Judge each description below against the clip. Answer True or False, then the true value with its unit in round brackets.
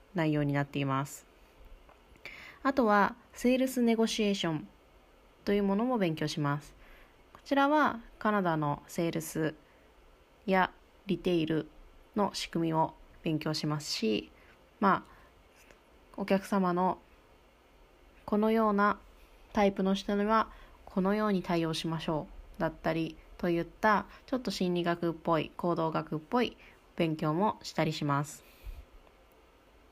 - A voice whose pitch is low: False (175 Hz)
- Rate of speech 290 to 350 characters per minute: False (260 characters per minute)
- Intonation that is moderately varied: True (4.7 semitones)